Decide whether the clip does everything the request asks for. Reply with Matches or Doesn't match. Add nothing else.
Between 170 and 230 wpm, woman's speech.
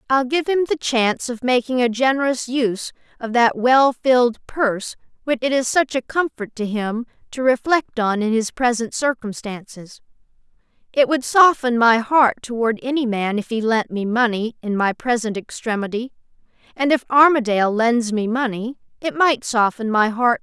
Matches